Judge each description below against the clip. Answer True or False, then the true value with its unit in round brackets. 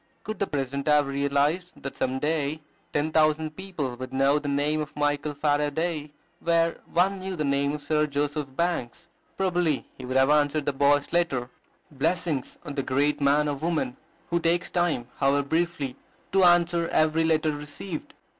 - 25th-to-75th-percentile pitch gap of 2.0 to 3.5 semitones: True (2.9 semitones)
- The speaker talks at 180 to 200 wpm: False (170 wpm)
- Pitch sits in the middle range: True (150 Hz)